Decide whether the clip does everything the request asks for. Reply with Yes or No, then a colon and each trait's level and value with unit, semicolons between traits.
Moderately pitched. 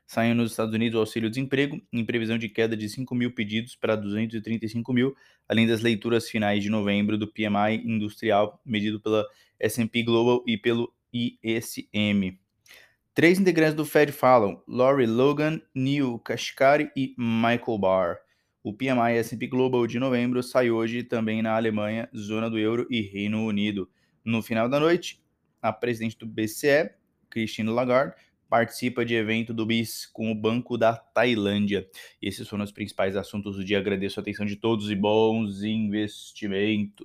No: low, 115 Hz